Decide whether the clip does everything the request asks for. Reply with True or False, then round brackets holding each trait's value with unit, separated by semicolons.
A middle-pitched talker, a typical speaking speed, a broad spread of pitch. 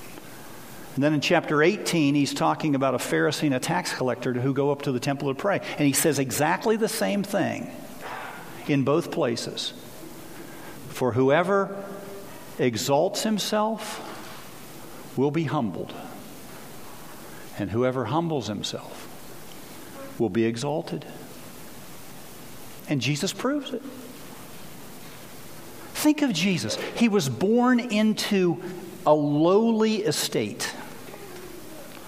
False (160 Hz; 110 wpm; 6.7 semitones)